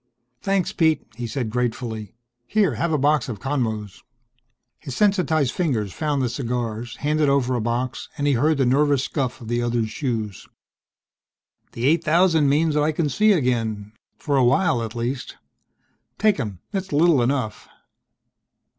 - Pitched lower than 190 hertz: Yes, low, 135 Hz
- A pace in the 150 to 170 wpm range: Yes, average, 155 wpm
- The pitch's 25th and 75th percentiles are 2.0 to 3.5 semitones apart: No, average, 4.6 semitones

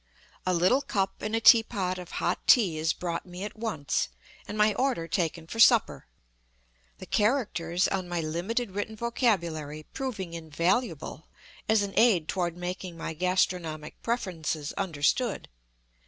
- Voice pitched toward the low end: No, medium, 185 Hz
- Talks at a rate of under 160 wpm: Yes, average, 150 wpm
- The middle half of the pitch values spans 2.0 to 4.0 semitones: No, average, 4.7 semitones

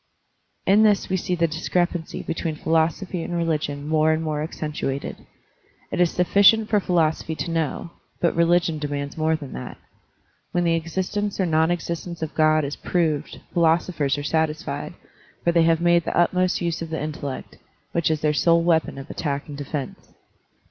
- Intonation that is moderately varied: No, narrow, 2.1 semitones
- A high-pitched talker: No, medium, 165 Hz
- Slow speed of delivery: No, average, 175 wpm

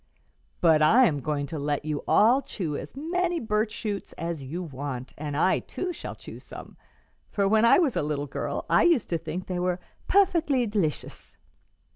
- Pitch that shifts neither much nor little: No, wide, 8.1 semitones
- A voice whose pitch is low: No, medium, 180 Hz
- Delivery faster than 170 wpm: Yes, average, 185 wpm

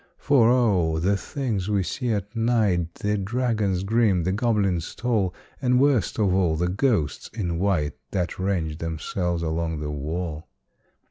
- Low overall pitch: Yes, very low, 95 Hz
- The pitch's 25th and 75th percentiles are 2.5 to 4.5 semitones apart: No, average, 5.0 semitones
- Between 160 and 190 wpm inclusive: No, average, 150 wpm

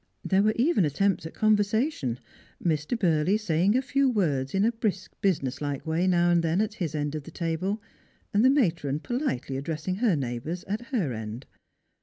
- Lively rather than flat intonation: Yes, wide, 6.0 semitones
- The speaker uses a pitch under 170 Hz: No, medium, 175 Hz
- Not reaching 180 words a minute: No, average, 190 wpm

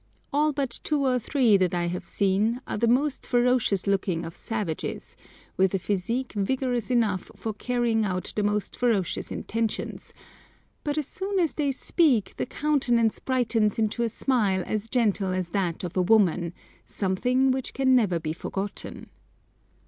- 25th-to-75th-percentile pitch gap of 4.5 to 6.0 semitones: Yes, average, 4.8 semitones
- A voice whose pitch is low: No, high, 225 Hz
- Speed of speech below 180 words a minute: Yes, average, 160 wpm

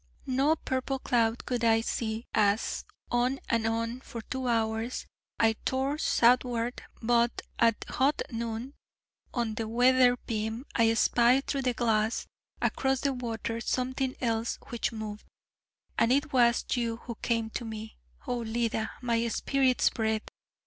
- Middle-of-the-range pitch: No, high, 235 Hz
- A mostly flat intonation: Yes, narrow, 2.1 semitones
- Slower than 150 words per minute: Yes, average, 140 wpm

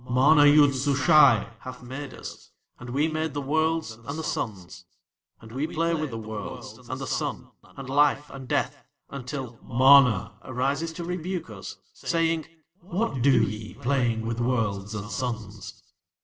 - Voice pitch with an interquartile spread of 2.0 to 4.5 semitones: No, average, 5.0 semitones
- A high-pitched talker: No, low, 135 Hz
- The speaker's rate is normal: Yes, average, 155 wpm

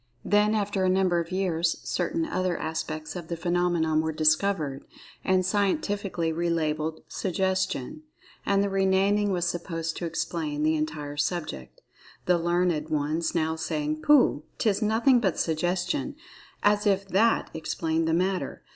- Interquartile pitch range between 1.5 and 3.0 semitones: No, average, 3.5 semitones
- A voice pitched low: No, medium, 175 Hz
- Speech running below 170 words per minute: Yes, average, 145 wpm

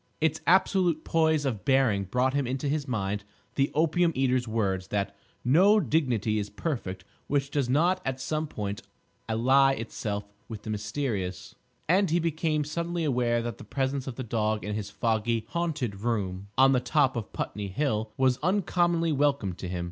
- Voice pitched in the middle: No, low, 130 Hz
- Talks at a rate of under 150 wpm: No, average, 170 wpm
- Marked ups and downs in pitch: Yes, wide, 6.2 semitones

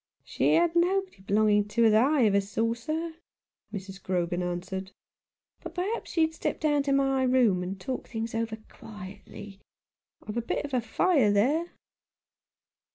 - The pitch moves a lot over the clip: Yes, wide, 6.6 semitones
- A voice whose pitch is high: Yes, high, 230 Hz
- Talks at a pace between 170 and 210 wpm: No, average, 160 wpm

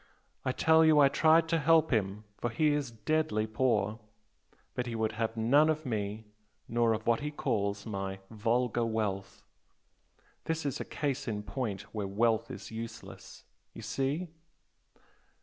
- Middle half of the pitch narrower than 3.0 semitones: No, average, 5.3 semitones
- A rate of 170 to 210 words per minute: No, average, 155 wpm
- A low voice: Yes, low, 115 Hz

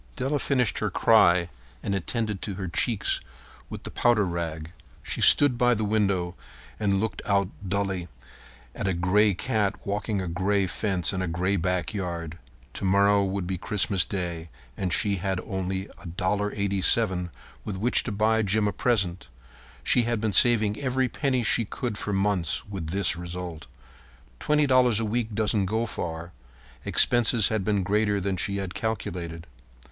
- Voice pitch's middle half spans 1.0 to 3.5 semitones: Yes, average, 3.2 semitones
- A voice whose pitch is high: No, low, 100 Hz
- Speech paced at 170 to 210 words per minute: No, average, 160 wpm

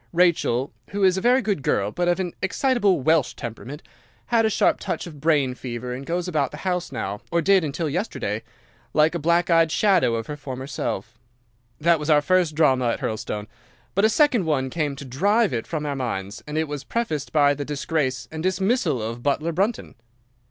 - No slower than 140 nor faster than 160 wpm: No, average, 190 wpm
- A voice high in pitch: No, medium, 155 Hz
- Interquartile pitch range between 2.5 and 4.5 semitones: No, wide, 5.6 semitones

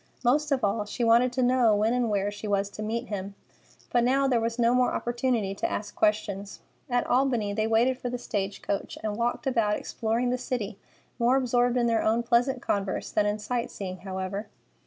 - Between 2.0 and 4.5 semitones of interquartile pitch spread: Yes, average, 3.1 semitones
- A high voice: Yes, high, 230 Hz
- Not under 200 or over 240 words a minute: Yes, fast, 205 wpm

